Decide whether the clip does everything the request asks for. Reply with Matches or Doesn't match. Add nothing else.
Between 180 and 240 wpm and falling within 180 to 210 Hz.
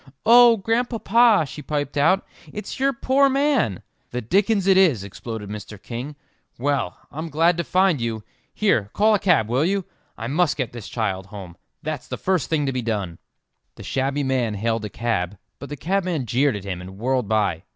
Doesn't match